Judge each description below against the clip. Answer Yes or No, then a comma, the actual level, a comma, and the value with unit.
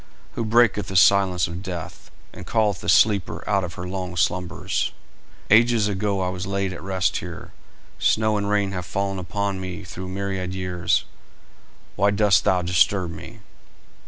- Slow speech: No, average, 160 wpm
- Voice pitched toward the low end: Yes, very low, 95 Hz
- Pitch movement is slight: Yes, narrow, 2.0 semitones